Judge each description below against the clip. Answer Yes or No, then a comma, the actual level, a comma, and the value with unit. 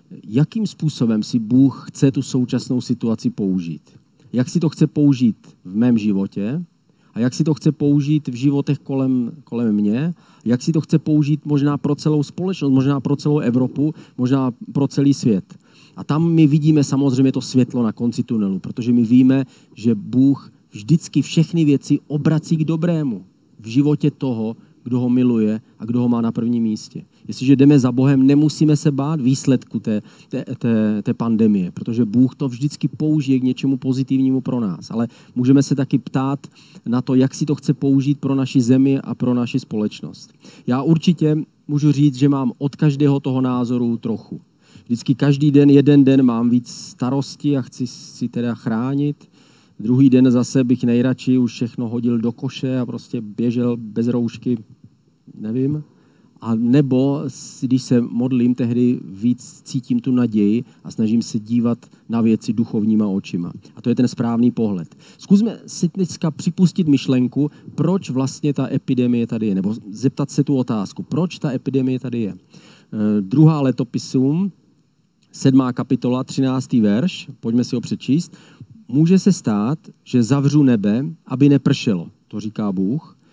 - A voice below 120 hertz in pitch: No, low, 135 Hz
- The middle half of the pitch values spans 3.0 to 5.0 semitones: Yes, average, 3.5 semitones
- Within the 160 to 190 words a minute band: Yes, average, 165 wpm